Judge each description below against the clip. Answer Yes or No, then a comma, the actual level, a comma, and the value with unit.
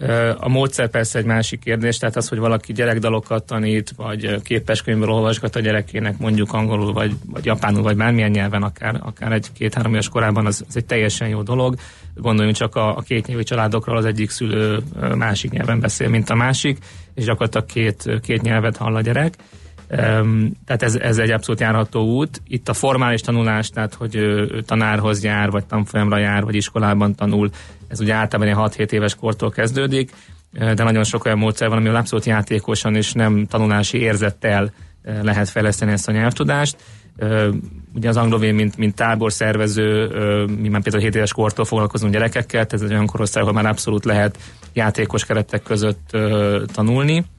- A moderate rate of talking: No, fast, 170 wpm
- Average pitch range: No, narrow, 1.5 semitones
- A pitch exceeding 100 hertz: Yes, low, 110 Hz